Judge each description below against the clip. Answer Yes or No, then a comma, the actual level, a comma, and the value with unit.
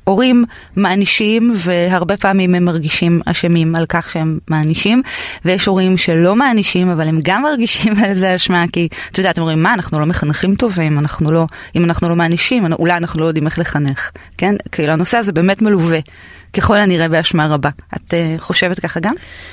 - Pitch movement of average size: Yes, average, 3.3 semitones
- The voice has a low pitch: No, medium, 175 Hz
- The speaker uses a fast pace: Yes, fast, 180 wpm